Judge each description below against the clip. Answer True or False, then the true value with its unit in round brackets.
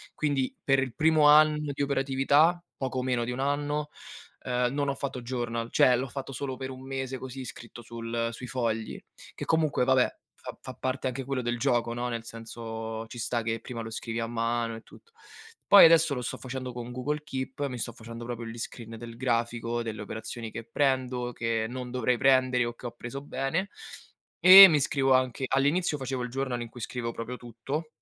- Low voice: True (125 Hz)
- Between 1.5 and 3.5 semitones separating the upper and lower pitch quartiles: True (2.6 semitones)